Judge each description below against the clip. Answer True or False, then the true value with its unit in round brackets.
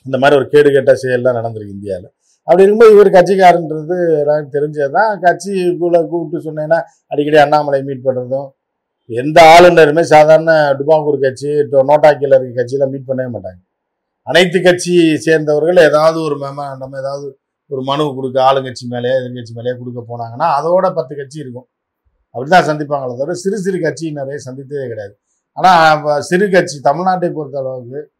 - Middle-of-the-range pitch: True (145 Hz)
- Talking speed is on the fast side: True (145 wpm)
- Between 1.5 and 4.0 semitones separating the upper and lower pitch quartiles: True (3.7 semitones)